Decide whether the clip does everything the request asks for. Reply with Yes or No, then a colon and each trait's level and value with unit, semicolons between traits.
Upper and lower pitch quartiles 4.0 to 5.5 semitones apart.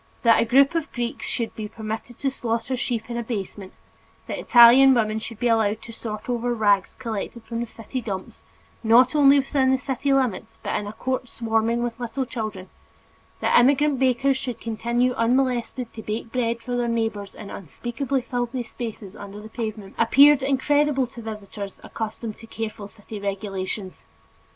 No: average, 2.8 semitones